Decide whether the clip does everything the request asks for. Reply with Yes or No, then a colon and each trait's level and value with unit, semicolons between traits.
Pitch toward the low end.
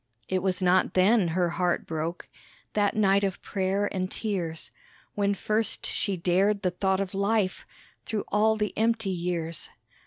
No: high, 190 Hz